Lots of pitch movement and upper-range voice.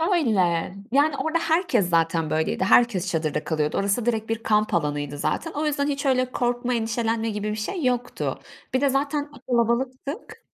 Yes: wide, 6.5 semitones; high, 235 Hz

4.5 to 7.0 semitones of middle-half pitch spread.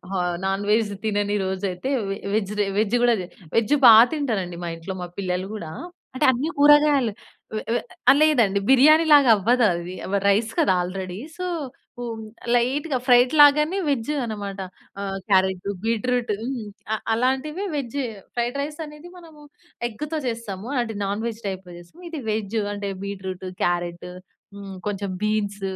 Yes: wide, 5.4 semitones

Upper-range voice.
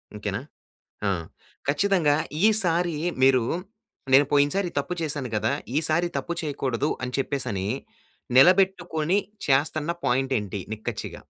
No: medium, 145 Hz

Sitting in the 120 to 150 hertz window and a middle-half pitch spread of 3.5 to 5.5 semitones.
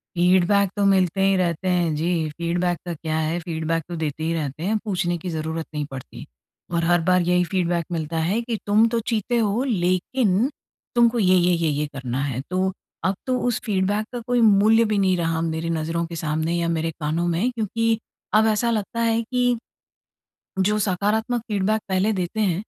No: medium, 180 Hz; average, 4.5 semitones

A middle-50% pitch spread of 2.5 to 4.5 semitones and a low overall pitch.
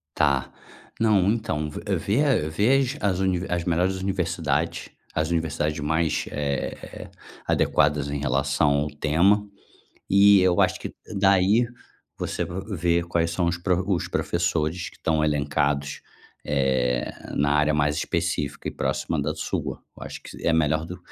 Yes: average, 4.0 semitones; very low, 80 Hz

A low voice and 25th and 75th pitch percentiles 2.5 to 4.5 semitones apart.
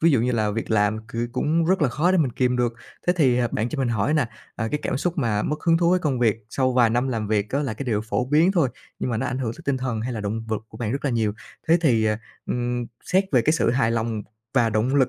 Yes: low, 125 Hz; average, 4.2 semitones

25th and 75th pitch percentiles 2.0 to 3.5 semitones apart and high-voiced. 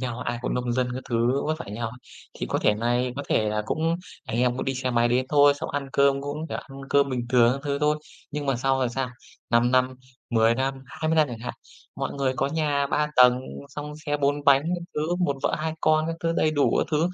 No: average, 3.1 semitones; low, 135 Hz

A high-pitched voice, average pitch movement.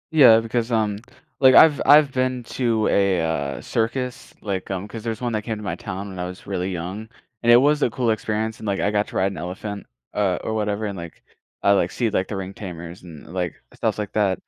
No: low, 105 Hz; average, 3.4 semitones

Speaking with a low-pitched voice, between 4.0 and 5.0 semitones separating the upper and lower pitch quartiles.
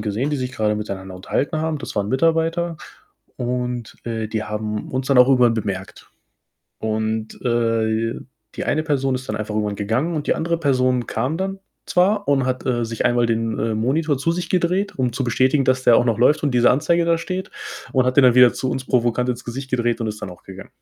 Yes: low, 125 Hz; average, 4.5 semitones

